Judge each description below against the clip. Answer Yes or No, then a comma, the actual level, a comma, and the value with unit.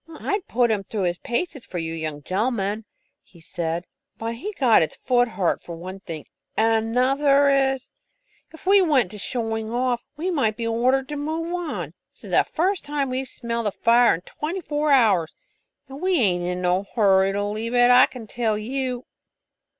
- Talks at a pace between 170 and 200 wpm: Yes, average, 190 wpm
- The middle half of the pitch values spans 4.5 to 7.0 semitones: Yes, wide, 5.4 semitones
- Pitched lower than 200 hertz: No, high, 235 Hz